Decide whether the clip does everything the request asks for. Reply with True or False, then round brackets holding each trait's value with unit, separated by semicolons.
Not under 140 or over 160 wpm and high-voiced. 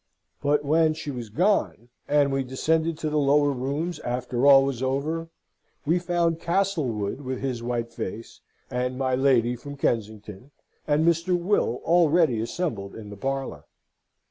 False (150 wpm; 140 Hz)